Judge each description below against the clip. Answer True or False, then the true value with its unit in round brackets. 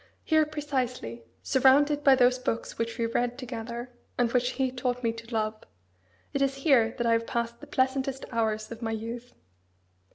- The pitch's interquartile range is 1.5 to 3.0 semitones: True (2.5 semitones)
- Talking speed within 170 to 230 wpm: True (175 wpm)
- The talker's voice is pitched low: False (245 Hz)